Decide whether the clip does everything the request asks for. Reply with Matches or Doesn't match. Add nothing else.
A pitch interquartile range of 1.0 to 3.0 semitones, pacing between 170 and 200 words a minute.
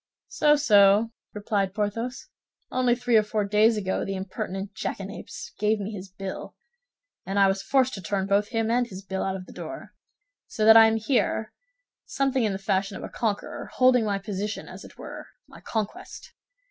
Matches